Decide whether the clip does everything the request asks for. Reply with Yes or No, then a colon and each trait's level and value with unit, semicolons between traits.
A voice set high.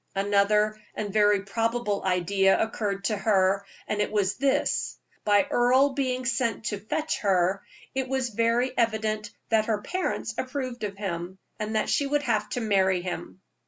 Yes: high, 215 Hz